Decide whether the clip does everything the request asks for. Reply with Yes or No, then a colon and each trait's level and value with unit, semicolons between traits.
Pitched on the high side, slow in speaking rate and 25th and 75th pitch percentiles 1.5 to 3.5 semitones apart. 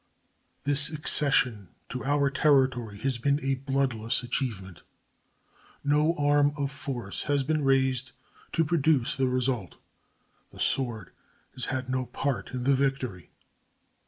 No: low, 135 Hz; slow, 130 wpm; narrow, 2.4 semitones